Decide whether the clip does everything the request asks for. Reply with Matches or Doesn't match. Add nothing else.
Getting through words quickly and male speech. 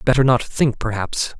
Doesn't match